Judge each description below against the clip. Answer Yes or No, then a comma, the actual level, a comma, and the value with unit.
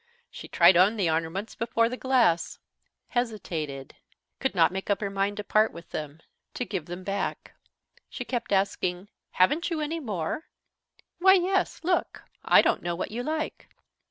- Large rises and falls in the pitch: Yes, wide, 6.1 semitones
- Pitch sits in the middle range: No, high, 205 Hz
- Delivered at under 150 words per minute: No, average, 165 wpm